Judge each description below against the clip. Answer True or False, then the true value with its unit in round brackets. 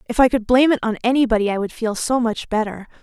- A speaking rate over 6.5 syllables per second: True (6.7 syllables/s)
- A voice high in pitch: True (230 Hz)